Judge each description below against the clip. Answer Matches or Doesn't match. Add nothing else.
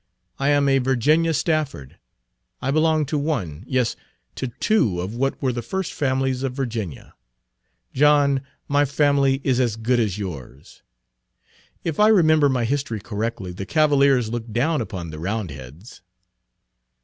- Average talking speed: Matches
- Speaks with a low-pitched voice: Matches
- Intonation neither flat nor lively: Matches